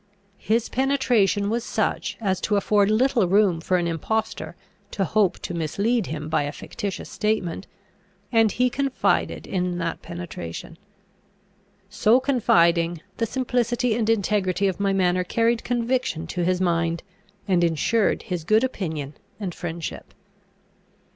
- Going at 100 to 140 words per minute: Yes, slow, 135 wpm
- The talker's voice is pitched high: Yes, high, 195 Hz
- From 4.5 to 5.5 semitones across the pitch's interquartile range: Yes, average, 4.9 semitones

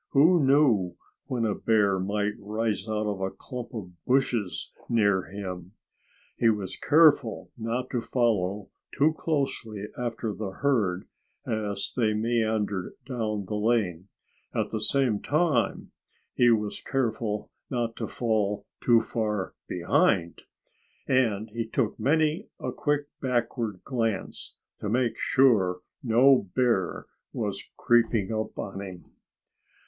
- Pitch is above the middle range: No, low, 110 Hz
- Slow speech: Yes, slow, 125 wpm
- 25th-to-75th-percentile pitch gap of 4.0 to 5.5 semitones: No, average, 3.5 semitones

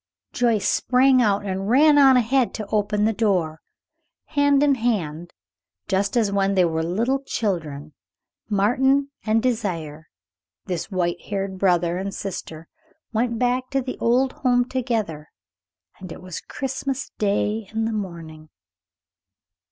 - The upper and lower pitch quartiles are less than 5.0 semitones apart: No, wide, 5.6 semitones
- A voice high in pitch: Yes, high, 210 Hz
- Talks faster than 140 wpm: No, slow, 135 wpm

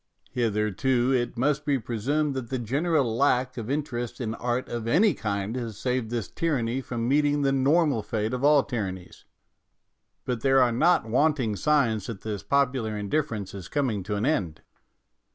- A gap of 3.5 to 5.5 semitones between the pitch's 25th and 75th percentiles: Yes, average, 4.1 semitones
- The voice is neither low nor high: No, low, 125 Hz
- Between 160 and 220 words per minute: Yes, average, 170 wpm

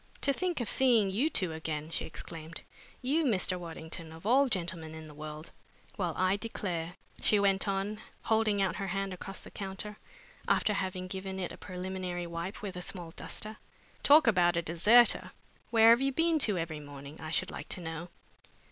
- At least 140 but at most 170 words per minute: No, average, 185 wpm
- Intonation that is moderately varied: Yes, average, 4.3 semitones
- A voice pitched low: No, high, 190 Hz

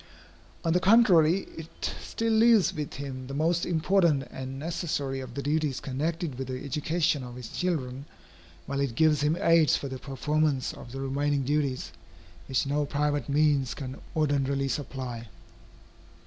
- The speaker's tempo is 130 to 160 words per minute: Yes, average, 155 wpm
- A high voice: No, medium, 145 Hz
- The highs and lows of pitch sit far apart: No, average, 3.1 semitones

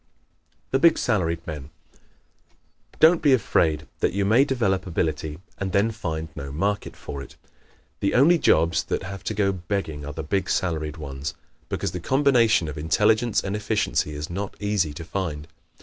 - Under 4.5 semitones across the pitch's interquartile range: No, average, 5.3 semitones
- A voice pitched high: No, very low, 95 Hz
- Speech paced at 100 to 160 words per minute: No, average, 170 wpm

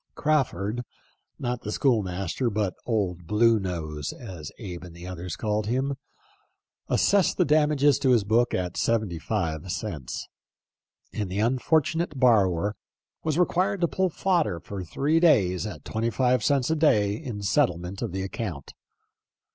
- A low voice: Yes, low, 110 Hz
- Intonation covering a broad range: Yes, wide, 6.7 semitones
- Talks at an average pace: Yes, average, 155 wpm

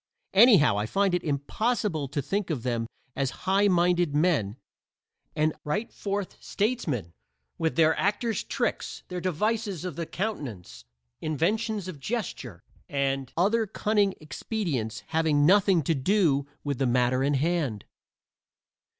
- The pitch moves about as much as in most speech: No, wide, 6.4 semitones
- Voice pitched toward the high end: No, medium, 165 Hz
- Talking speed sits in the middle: No, slow, 130 wpm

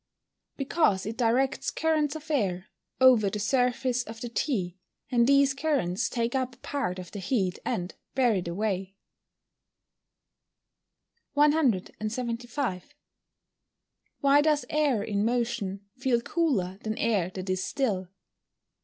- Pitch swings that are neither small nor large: No, wide, 5.7 semitones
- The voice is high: Yes, high, 235 Hz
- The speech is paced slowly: Yes, slow, 125 wpm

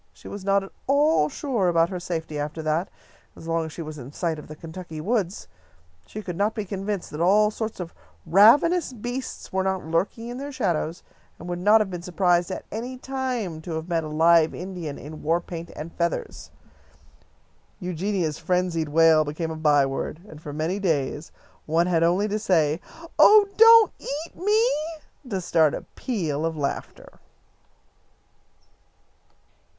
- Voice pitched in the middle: Yes, medium, 175 Hz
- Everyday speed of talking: Yes, average, 170 wpm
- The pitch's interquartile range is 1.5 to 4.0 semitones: No, average, 4.7 semitones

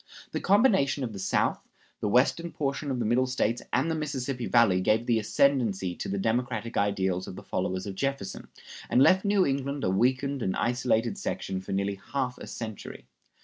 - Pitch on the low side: Yes, low, 120 Hz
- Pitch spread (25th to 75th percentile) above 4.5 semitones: Yes, wide, 5.4 semitones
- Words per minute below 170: No, average, 190 wpm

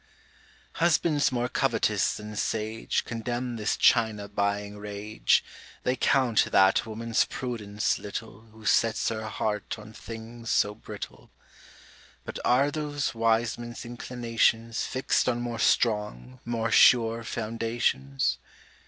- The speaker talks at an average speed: No, slow, 120 wpm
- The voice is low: Yes, low, 115 Hz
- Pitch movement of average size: No, narrow, 2.1 semitones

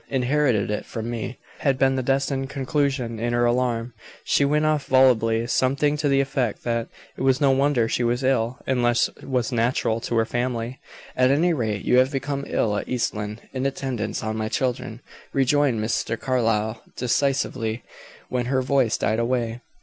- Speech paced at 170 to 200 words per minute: Yes, average, 175 wpm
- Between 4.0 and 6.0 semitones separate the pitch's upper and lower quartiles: No, average, 2.7 semitones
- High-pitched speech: No, low, 125 Hz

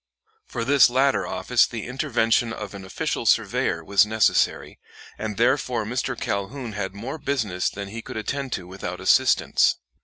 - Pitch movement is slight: No, average, 4.5 semitones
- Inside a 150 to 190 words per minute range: Yes, average, 155 wpm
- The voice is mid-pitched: No, low, 115 Hz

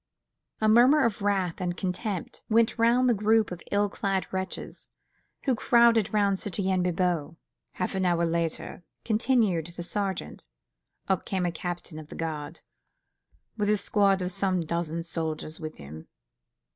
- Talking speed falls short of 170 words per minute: Yes, average, 150 wpm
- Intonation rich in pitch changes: No, average, 3.8 semitones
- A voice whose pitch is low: No, high, 190 Hz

